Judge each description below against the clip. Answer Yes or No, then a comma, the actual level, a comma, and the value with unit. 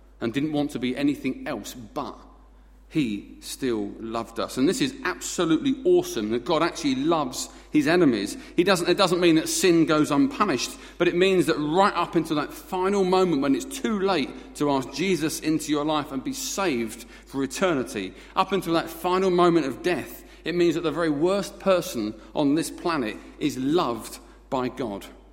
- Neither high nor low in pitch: Yes, medium, 175 Hz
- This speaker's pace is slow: No, average, 185 wpm